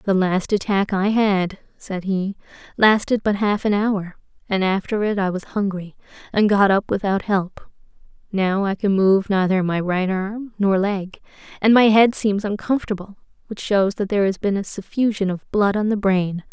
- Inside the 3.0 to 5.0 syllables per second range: Yes, 4.7 syllables/s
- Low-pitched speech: No, high, 200 Hz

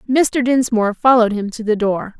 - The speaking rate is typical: Yes, average, 190 wpm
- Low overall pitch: No, high, 230 Hz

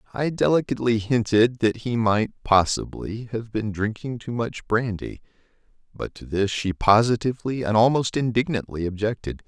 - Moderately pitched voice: No, low, 110 Hz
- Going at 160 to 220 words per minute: No, average, 140 wpm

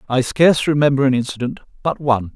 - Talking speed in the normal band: Yes, average, 180 wpm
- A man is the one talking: Yes, male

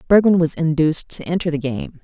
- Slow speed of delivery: No, fast, 205 wpm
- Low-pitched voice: No, medium, 160 Hz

